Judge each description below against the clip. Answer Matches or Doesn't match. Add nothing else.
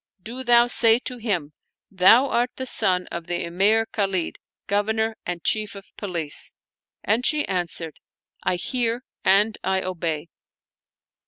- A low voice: Doesn't match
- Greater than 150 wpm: Doesn't match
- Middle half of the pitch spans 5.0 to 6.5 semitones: Doesn't match